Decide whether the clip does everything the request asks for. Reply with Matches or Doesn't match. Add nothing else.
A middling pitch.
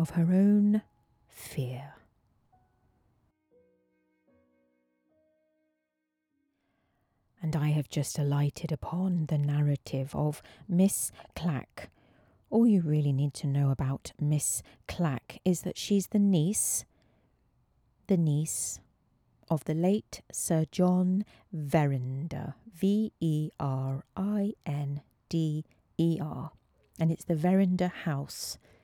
Matches